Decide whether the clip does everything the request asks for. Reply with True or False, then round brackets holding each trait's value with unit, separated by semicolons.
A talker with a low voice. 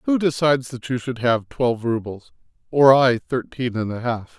True (125 Hz)